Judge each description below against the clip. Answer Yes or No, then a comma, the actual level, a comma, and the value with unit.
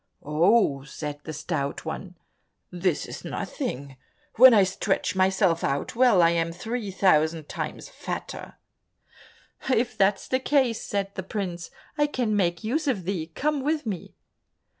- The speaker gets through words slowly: No, average, 145 wpm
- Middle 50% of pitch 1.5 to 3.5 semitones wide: No, wide, 5.5 semitones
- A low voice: No, high, 190 Hz